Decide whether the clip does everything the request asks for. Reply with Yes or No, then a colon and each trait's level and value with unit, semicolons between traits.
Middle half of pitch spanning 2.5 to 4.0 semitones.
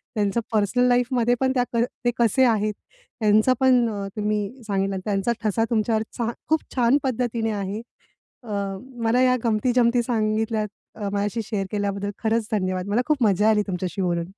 Yes: average, 2.9 semitones